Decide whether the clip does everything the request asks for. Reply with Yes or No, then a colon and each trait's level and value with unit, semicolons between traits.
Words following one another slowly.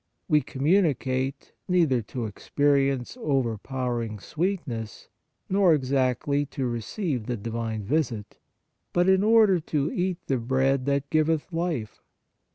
Yes: slow, 120 wpm